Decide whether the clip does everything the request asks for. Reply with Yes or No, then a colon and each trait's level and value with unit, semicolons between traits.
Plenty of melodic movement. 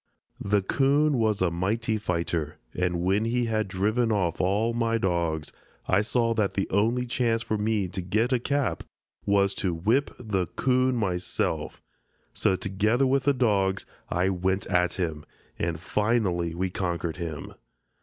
No: average, 4.2 semitones